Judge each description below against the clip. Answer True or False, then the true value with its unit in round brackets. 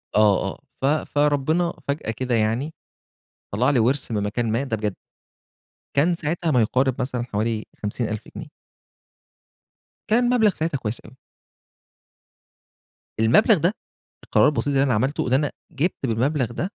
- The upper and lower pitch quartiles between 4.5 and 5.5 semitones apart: True (5.1 semitones)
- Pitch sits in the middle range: False (130 Hz)